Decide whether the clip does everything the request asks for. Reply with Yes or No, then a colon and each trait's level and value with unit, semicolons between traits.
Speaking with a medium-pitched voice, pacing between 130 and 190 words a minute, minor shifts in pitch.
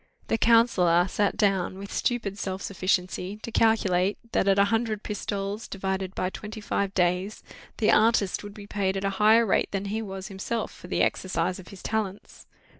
No: high, 200 Hz; average, 185 wpm; narrow, 2.1 semitones